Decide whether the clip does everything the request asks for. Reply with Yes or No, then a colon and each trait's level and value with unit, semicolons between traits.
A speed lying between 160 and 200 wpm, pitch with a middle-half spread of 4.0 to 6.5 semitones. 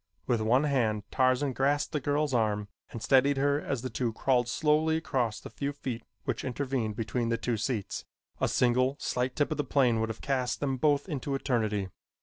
No: average, 195 wpm; average, 3.5 semitones